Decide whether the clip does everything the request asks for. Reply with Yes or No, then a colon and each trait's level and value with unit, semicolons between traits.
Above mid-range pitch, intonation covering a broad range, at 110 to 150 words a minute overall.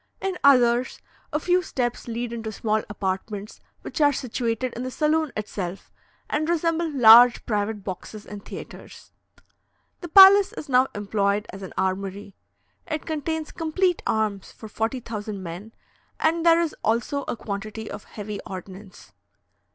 Yes: high, 230 Hz; wide, 6.7 semitones; average, 145 wpm